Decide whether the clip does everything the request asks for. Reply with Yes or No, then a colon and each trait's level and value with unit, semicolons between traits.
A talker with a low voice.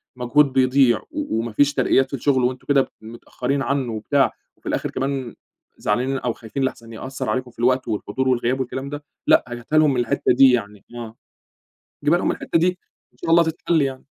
Yes: low, 130 Hz